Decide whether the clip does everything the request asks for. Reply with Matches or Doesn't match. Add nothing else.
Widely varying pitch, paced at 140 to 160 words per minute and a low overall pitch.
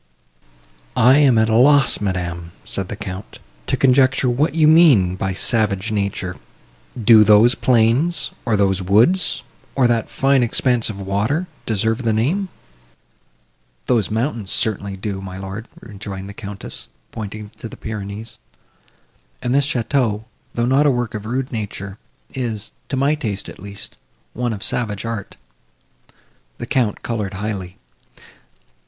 Doesn't match